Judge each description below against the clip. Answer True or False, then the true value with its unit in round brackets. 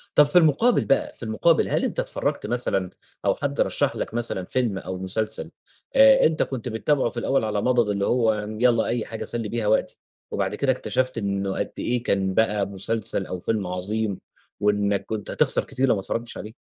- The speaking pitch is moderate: False (110 Hz)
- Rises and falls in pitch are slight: False (3.5 semitones)